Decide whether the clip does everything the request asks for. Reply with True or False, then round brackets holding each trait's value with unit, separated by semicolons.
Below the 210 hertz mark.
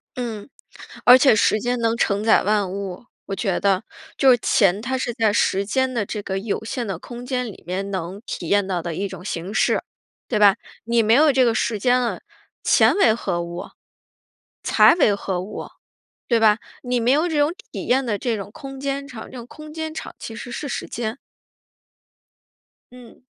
False (225 Hz)